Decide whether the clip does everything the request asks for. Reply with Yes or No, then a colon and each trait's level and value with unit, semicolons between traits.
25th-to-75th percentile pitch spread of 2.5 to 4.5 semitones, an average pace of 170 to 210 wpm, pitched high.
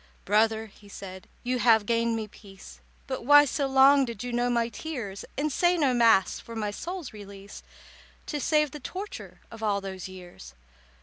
No: average, 5.0 semitones; average, 180 wpm; high, 230 Hz